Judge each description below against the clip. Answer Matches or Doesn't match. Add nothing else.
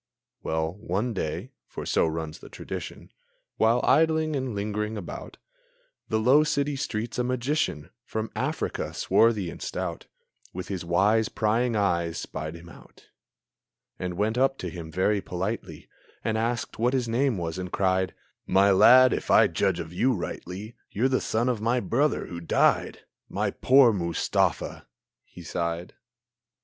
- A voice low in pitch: Matches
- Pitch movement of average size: Doesn't match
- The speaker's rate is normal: Matches